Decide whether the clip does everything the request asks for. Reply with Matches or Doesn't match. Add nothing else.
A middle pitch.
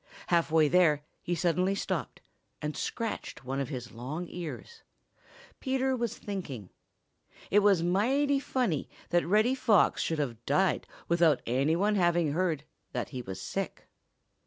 Matches